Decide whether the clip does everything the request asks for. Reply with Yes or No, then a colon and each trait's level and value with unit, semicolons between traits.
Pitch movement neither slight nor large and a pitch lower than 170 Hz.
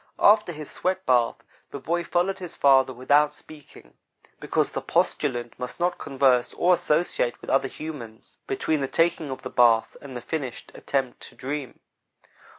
Yes: average, 4.9 semitones; medium, 140 Hz